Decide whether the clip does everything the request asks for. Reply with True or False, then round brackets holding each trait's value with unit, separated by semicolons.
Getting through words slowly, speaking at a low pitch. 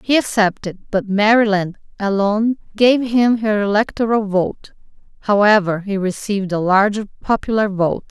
False (125 wpm; 210 Hz)